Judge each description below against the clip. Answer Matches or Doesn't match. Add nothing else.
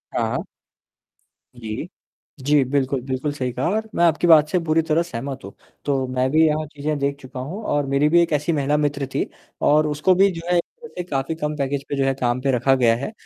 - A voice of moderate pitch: Matches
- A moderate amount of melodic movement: Matches